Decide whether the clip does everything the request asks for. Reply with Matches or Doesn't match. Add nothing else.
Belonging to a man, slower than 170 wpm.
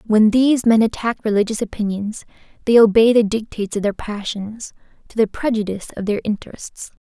Doesn't match